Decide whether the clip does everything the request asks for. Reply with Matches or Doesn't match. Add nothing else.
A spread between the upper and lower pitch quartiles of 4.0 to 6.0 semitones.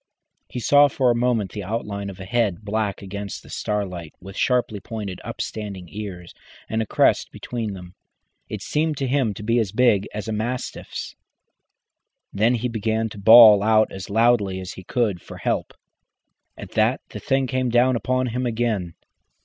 Doesn't match